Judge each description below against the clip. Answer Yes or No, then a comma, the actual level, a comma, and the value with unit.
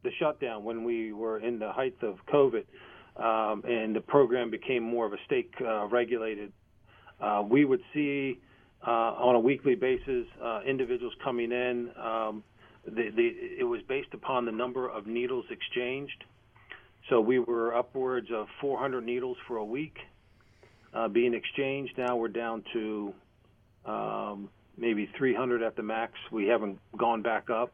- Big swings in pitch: No, average, 3.4 semitones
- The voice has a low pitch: Yes, low, 120 Hz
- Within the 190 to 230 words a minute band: No, average, 160 wpm